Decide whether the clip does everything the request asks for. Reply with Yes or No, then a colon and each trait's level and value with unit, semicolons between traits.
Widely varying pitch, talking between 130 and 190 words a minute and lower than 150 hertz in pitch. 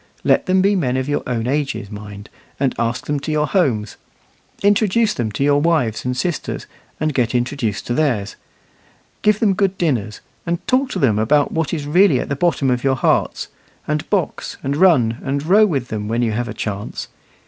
No: wide, 6.4 semitones; average, 200 wpm; medium, 140 Hz